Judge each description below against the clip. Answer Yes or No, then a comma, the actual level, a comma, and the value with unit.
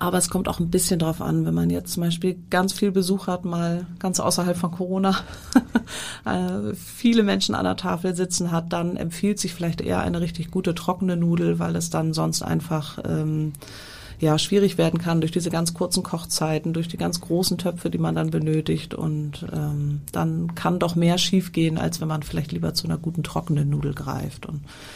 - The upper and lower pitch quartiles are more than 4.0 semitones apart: No, average, 3.6 semitones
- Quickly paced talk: Yes, fast, 195 wpm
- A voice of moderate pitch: Yes, medium, 170 Hz